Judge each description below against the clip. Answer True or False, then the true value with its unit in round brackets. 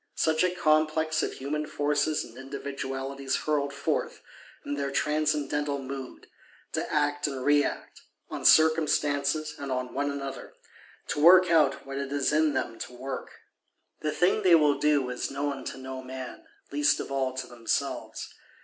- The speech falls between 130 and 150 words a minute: False (160 wpm)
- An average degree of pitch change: False (2.0 semitones)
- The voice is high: False (145 Hz)